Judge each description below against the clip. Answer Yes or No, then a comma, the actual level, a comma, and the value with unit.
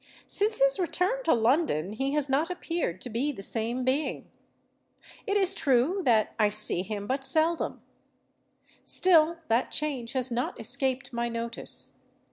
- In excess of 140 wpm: Yes, average, 150 wpm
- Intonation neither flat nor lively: No, wide, 6.3 semitones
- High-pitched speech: Yes, very high, 265 Hz